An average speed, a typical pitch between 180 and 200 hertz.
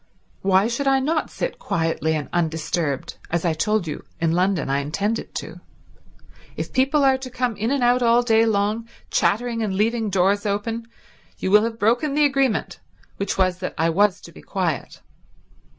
No: average, 180 wpm; high, 210 Hz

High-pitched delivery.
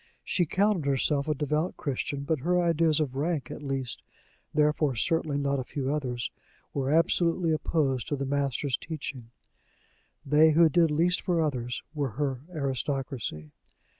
No: medium, 145 Hz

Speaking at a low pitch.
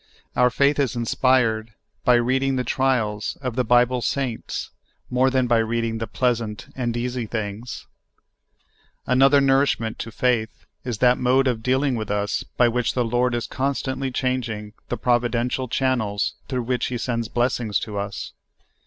Yes: low, 125 Hz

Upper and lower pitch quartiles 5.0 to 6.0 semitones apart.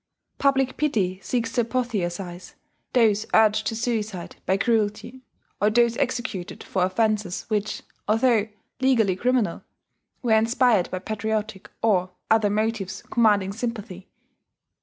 No: average, 3.3 semitones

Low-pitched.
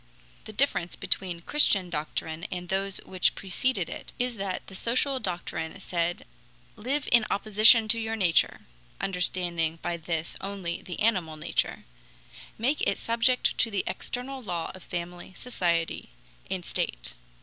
No: high, 190 Hz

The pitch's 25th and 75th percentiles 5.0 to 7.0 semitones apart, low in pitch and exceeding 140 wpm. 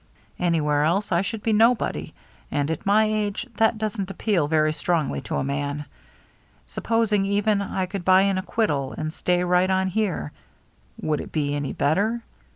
No: average, 5.3 semitones; medium, 185 Hz; average, 165 wpm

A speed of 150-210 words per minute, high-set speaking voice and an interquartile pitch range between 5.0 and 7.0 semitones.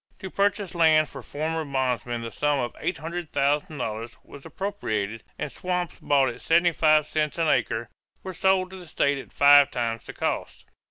No: average, 170 wpm; medium, 150 Hz; average, 5.3 semitones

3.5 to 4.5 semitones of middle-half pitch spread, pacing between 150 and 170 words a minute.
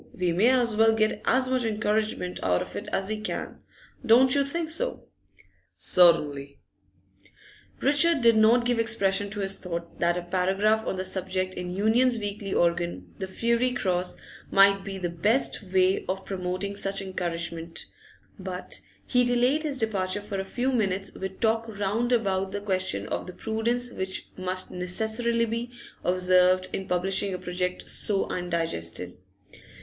Yes: average, 3.8 semitones; average, 160 wpm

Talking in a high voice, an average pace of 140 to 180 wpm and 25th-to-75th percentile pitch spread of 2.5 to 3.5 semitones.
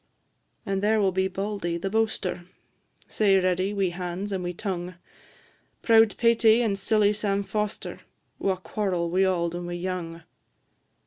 Yes: high, 195 Hz; average, 145 wpm; average, 2.8 semitones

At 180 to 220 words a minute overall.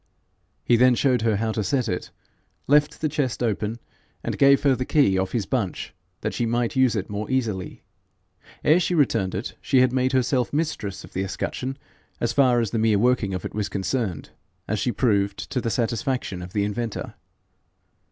Yes: average, 190 wpm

